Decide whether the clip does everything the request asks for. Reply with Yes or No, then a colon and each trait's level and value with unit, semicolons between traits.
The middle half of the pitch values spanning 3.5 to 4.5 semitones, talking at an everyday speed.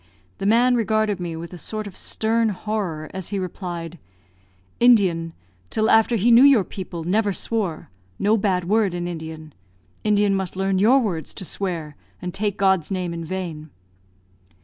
Yes: average, 3.9 semitones; average, 165 wpm